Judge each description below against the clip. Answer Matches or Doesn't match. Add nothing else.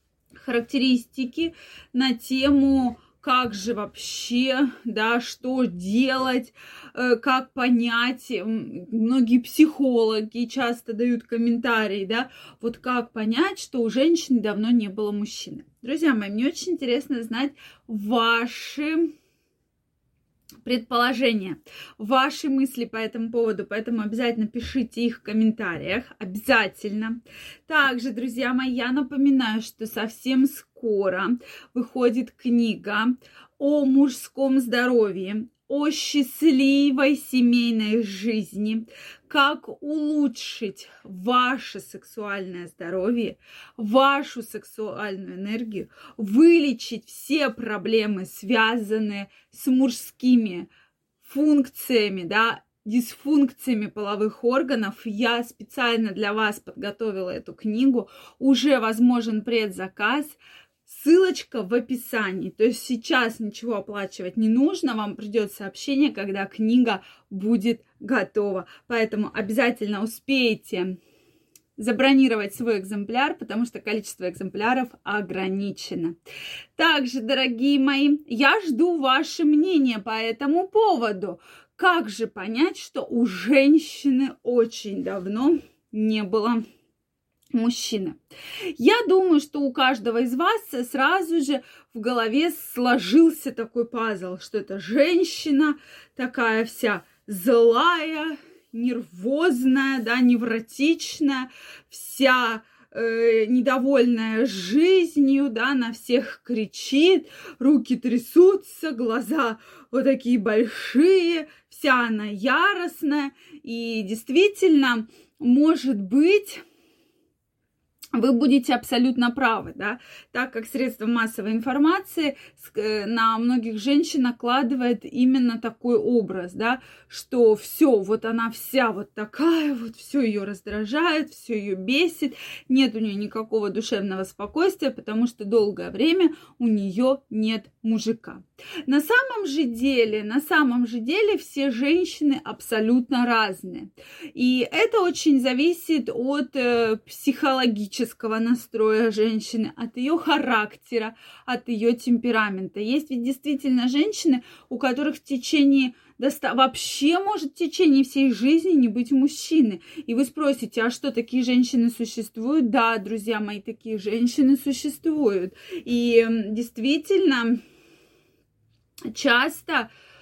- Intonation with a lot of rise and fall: Doesn't match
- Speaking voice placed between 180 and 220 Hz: Doesn't match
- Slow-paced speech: Matches